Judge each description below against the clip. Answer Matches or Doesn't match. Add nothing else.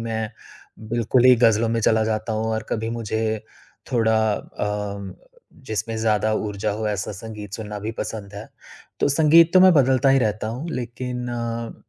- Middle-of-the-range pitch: Doesn't match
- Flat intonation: Matches